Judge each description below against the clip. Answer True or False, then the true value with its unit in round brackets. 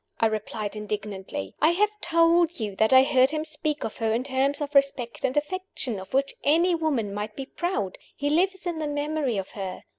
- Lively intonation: True (6.4 semitones)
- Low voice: False (275 Hz)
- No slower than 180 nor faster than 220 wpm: True (205 wpm)